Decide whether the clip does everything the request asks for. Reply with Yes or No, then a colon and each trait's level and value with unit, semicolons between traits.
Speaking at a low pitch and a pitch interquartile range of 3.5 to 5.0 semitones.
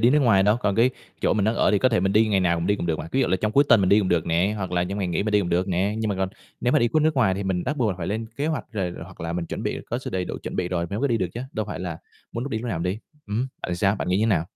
Yes: low, 100 Hz; average, 3.8 semitones